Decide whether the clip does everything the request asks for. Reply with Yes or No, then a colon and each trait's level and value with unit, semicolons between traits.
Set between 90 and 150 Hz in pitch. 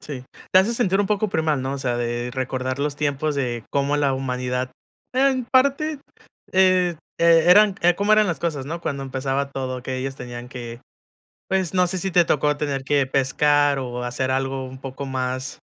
Yes: medium, 140 Hz